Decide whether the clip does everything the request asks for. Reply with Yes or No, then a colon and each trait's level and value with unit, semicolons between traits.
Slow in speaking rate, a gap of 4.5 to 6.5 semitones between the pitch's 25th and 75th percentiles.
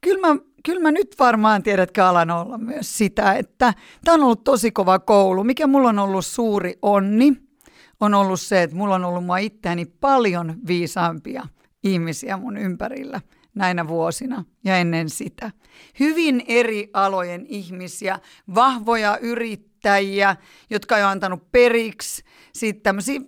No: average, 140 wpm; average, 4.9 semitones